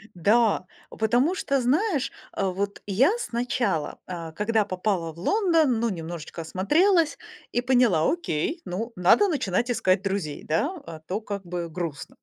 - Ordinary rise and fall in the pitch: No, wide, 6.6 semitones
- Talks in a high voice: Yes, high, 205 Hz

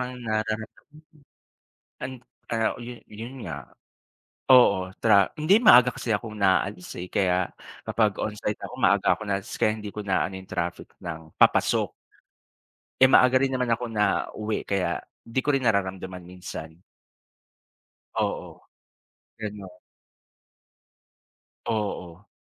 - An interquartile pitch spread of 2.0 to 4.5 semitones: Yes, average, 3.9 semitones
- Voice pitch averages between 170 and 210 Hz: No, low, 105 Hz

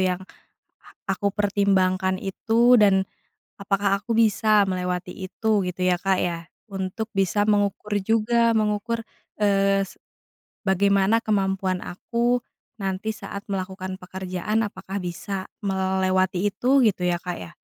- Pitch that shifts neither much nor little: No, narrow, 2.2 semitones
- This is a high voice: Yes, high, 195 Hz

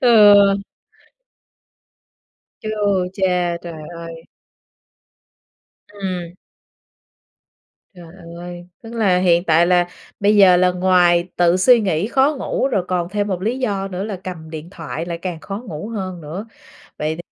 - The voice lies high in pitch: No, medium, 180 Hz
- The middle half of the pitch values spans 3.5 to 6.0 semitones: No, average, 2.9 semitones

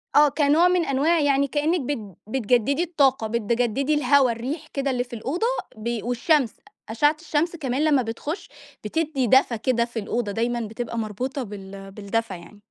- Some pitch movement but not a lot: Yes, average, 4.5 semitones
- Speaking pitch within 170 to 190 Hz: No, very high, 255 Hz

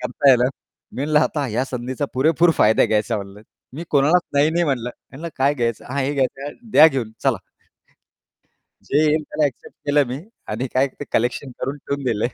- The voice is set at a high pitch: No, low, 135 Hz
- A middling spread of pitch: Yes, average, 3.1 semitones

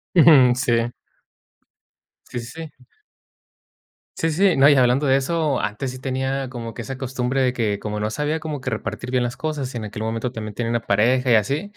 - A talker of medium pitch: No, low, 130 Hz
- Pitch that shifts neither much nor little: Yes, average, 3.0 semitones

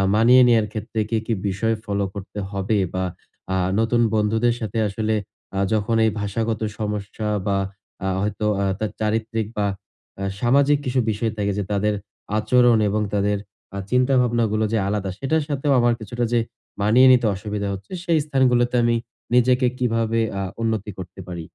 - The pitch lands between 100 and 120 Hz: Yes, low, 110 Hz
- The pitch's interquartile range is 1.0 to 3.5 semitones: Yes, average, 2.7 semitones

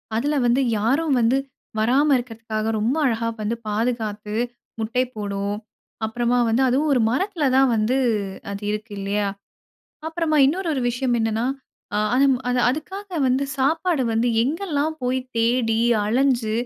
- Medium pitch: No, high, 245 Hz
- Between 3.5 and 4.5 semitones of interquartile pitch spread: Yes, average, 3.9 semitones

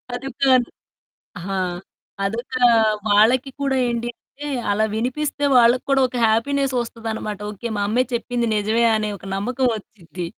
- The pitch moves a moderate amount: Yes, average, 3.3 semitones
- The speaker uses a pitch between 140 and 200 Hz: No, high, 235 Hz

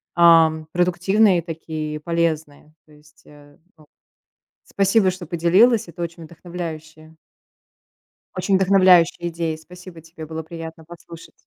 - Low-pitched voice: No, medium, 170 Hz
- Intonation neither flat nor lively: No, narrow, 2.1 semitones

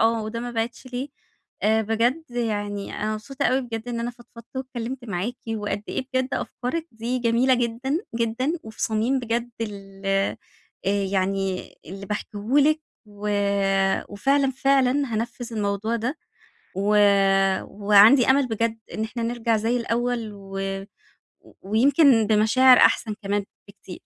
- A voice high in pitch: Yes, high, 230 Hz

